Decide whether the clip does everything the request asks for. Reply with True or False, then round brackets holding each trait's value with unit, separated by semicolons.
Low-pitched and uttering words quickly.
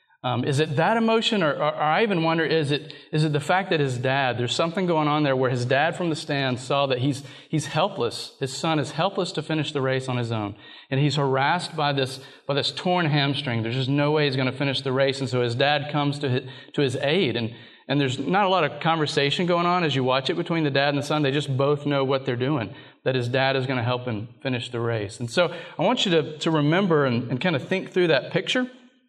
False (145 Hz; 270 wpm)